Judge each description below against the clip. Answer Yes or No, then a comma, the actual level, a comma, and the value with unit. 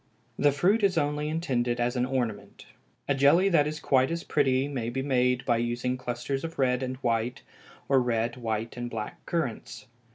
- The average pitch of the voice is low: Yes, low, 130 Hz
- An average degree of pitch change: Yes, average, 3.2 semitones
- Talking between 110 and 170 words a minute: No, average, 185 wpm